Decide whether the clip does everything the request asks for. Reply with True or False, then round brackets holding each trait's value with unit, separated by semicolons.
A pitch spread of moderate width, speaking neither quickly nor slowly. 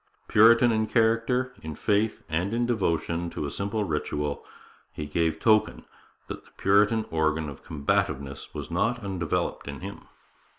False (6.2 semitones; 145 wpm)